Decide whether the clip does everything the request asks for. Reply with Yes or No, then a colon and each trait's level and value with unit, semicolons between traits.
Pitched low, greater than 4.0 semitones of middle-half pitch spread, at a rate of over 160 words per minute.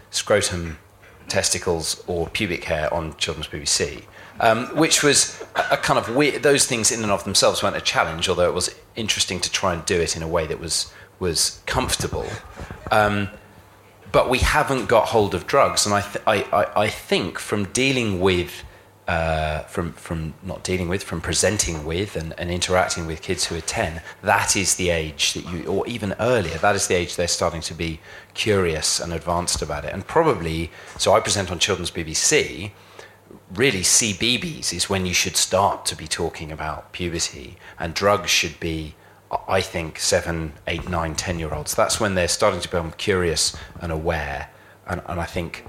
No: very low, 90 Hz; average, 3.7 semitones; average, 190 wpm